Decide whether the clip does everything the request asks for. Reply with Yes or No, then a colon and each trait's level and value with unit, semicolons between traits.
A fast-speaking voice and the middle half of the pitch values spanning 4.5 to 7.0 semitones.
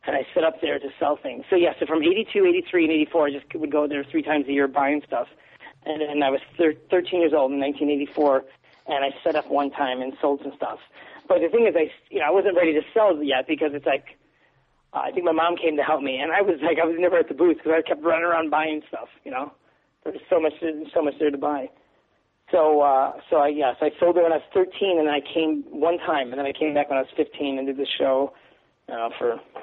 No: fast, 280 wpm; average, 3.1 semitones